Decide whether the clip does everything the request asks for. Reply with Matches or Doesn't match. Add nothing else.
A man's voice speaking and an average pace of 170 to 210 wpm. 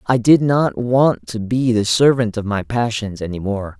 Matches